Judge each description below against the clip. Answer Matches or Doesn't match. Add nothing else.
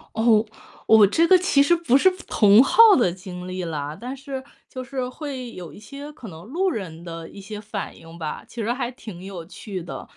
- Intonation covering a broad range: Matches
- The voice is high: Matches